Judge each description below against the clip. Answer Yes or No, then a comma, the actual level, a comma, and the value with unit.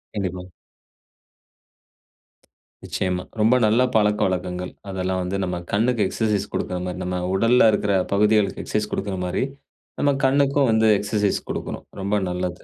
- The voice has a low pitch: Yes, low, 100 Hz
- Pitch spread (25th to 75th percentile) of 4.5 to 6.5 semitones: No, average, 3.2 semitones